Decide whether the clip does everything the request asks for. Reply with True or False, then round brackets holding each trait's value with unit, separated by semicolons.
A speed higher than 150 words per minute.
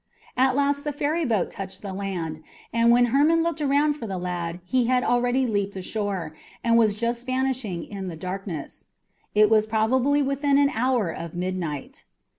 True (170 wpm)